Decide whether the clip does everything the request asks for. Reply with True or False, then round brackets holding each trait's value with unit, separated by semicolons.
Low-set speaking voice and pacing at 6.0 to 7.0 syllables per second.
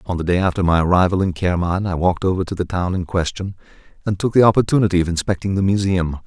True (90 Hz; 6.8 syllables/s)